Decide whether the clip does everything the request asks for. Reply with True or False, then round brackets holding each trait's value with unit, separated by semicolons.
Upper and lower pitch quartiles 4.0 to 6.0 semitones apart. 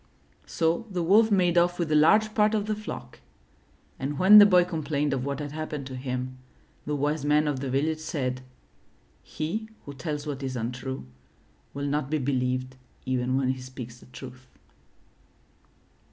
True (4.6 semitones)